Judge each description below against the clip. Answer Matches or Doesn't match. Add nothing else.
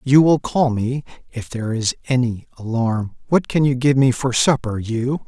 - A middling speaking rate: Matches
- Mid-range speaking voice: Doesn't match